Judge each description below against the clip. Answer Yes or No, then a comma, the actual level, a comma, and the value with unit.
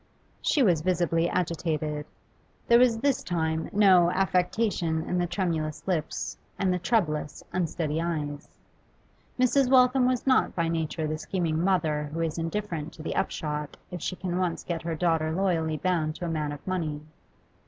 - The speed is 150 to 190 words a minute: Yes, average, 165 wpm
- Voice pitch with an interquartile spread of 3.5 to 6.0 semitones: No, average, 2.9 semitones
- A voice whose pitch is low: No, medium, 170 Hz